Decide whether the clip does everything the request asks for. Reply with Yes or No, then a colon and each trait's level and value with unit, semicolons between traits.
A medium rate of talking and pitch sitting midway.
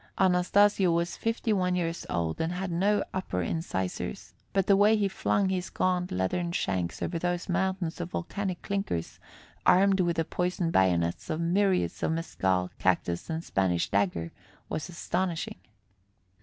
Yes: average, 150 wpm; medium, 175 Hz